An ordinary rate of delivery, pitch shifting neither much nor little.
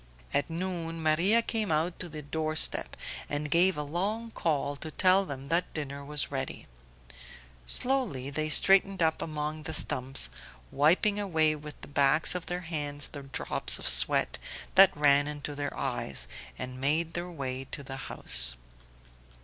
Yes: average, 160 wpm; average, 3.6 semitones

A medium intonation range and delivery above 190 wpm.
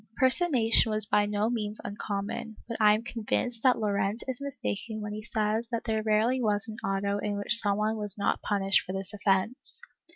No: narrow, 2.0 semitones; average, 200 wpm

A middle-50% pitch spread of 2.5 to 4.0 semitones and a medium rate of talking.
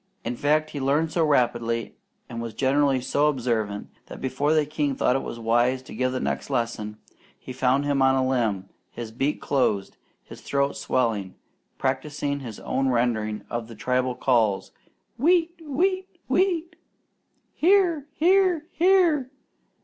No: average, 4.6 semitones; average, 150 wpm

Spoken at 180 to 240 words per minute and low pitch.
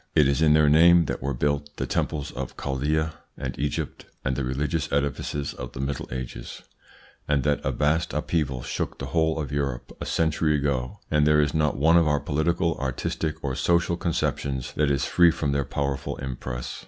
Yes: average, 190 wpm; very low, 75 Hz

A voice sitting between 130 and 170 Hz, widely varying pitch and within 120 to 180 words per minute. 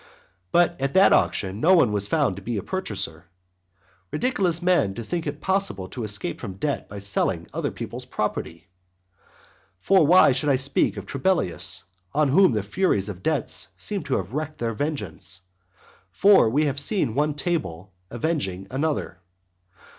Yes: low, 135 Hz; wide, 8.6 semitones; average, 160 wpm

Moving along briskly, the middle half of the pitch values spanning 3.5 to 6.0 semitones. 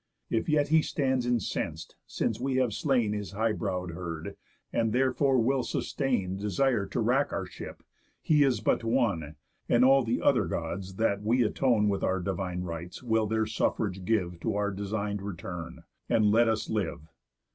No: average, 170 wpm; average, 4.4 semitones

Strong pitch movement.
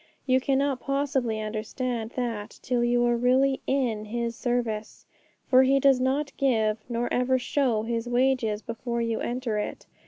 No: narrow, 2.5 semitones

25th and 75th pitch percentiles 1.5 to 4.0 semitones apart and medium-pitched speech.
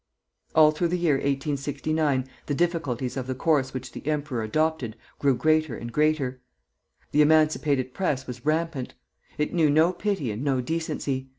Yes: average, 3.2 semitones; medium, 145 Hz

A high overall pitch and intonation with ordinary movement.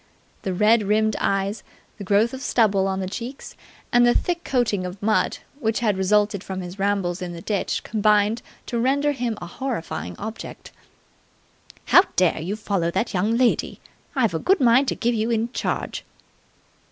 Yes: high, 215 Hz; average, 3.6 semitones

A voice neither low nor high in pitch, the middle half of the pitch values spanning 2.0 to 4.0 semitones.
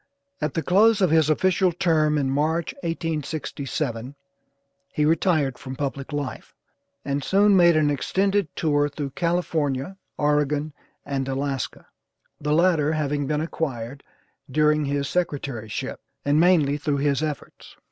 Yes: medium, 150 Hz; average, 2.8 semitones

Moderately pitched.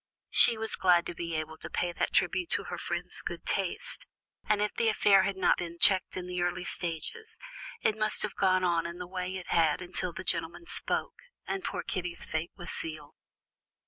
Yes: medium, 180 Hz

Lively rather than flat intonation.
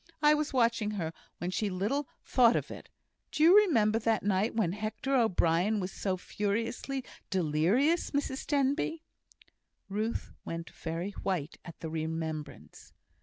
Yes: wide, 7.0 semitones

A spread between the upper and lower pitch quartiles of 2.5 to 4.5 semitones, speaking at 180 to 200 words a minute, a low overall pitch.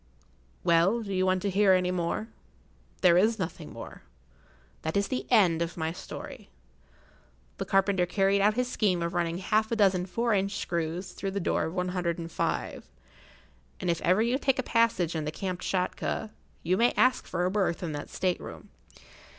No: average, 3.2 semitones; average, 190 wpm; medium, 185 Hz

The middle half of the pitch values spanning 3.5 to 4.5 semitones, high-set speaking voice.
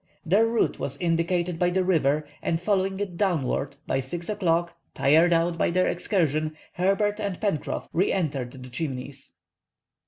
No: average, 3.8 semitones; medium, 170 Hz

